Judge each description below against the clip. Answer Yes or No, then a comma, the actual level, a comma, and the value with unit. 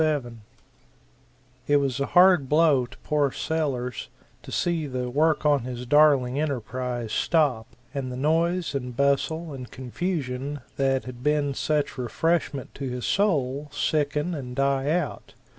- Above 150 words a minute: No, average, 140 wpm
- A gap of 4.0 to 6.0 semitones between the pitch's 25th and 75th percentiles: No, average, 3.3 semitones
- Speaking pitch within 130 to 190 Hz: Yes, medium, 140 Hz